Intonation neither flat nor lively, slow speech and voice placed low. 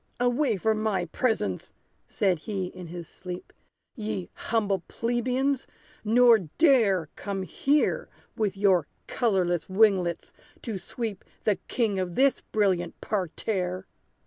No: average, 4.0 semitones; slow, 120 wpm; high, 200 Hz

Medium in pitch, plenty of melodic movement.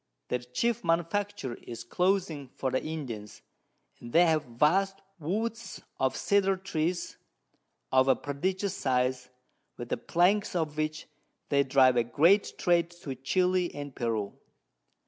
Yes: medium, 155 Hz; wide, 6.1 semitones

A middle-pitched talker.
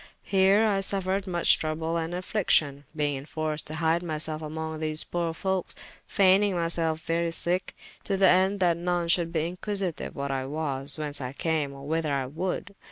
Yes: medium, 165 Hz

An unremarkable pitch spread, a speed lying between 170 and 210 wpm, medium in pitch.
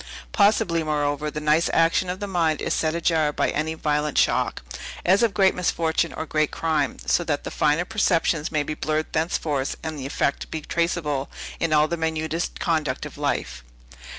No: narrow, 2.0 semitones; average, 180 wpm; medium, 160 Hz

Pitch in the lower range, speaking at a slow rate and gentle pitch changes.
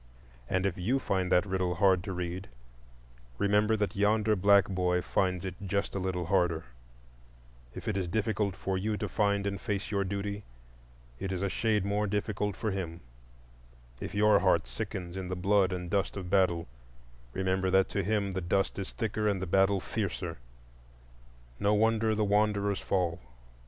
No: low, 100 Hz; average, 170 wpm; narrow, 2.0 semitones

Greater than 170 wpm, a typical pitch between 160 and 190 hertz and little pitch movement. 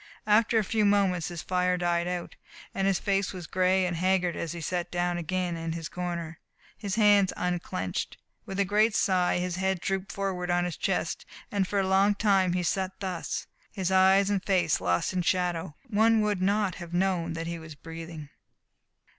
Yes: average, 190 wpm; medium, 185 Hz; narrow, 2.2 semitones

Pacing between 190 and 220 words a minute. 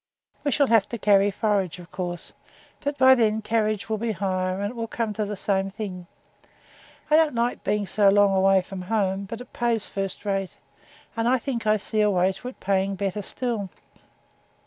Yes: average, 195 wpm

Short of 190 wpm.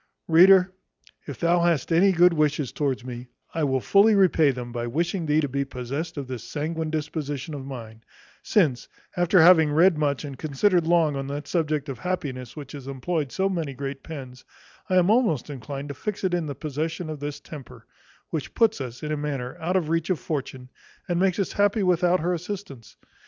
No: average, 200 wpm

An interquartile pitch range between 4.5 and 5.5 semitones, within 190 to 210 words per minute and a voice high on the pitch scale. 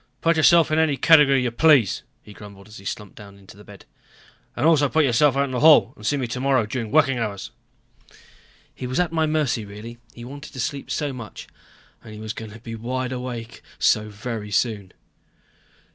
No: average, 5.0 semitones; average, 200 wpm; low, 125 Hz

